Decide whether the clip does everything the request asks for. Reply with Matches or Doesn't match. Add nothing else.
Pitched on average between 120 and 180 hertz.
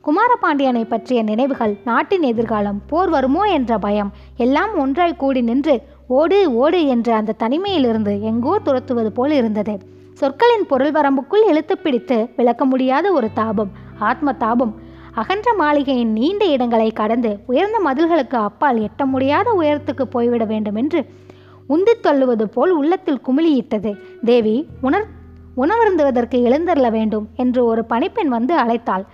Doesn't match